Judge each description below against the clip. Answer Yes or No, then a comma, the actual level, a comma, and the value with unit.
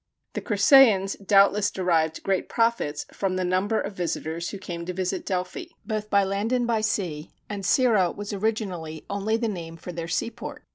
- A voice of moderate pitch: No, high, 195 Hz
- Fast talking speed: No, average, 180 wpm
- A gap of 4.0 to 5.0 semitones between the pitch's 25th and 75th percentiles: No, average, 3.3 semitones